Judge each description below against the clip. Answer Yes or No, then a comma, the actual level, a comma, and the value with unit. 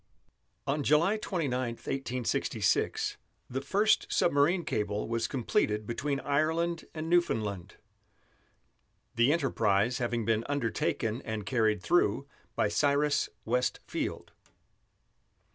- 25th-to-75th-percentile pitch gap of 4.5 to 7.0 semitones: Yes, average, 5.3 semitones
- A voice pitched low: Yes, low, 130 Hz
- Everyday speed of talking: No, slow, 100 wpm